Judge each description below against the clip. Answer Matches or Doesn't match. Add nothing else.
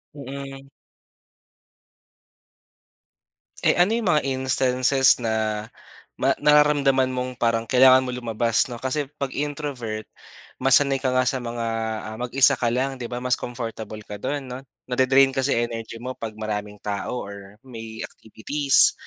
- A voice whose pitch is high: Doesn't match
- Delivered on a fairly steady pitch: Doesn't match